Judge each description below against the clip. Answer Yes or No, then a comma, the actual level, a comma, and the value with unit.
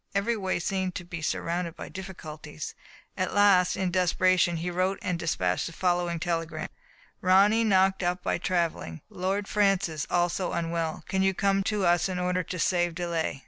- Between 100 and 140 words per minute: No, average, 170 wpm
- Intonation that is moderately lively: No, narrow, 2.0 semitones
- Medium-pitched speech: Yes, medium, 180 Hz